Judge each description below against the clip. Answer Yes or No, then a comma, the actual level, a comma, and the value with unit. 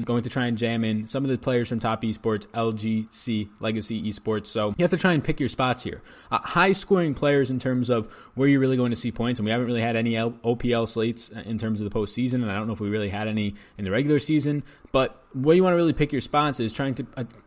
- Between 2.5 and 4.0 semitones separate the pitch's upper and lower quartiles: Yes, average, 3.4 semitones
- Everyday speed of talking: No, fast, 270 wpm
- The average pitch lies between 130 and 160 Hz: No, low, 120 Hz